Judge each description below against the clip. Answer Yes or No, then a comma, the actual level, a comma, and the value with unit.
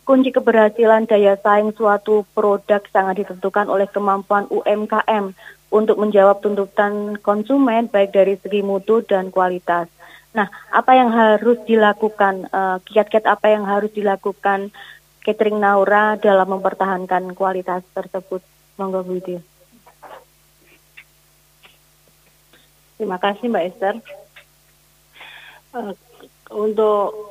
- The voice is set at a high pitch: Yes, high, 205 Hz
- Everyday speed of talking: Yes, average, 100 wpm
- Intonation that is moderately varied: No, narrow, 1.8 semitones